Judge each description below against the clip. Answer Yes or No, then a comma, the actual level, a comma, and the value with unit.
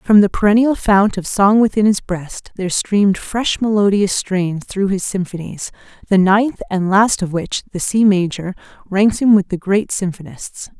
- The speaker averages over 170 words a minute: Yes, average, 180 wpm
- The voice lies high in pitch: Yes, high, 195 Hz